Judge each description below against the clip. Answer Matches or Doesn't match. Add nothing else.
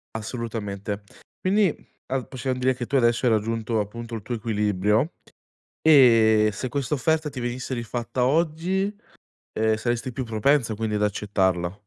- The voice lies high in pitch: Doesn't match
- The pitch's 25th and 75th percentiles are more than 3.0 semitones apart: Matches